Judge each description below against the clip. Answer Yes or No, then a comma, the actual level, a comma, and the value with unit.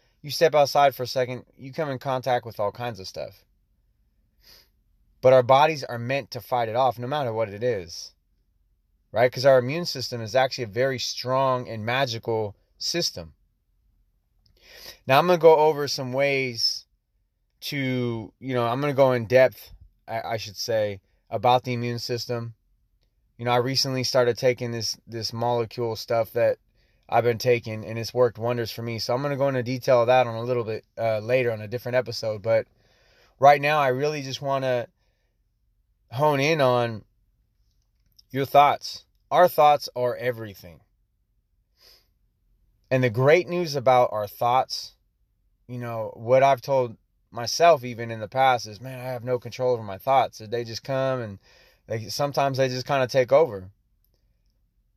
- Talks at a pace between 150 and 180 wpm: Yes, average, 175 wpm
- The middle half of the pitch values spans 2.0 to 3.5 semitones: Yes, average, 3.0 semitones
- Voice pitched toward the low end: Yes, low, 120 Hz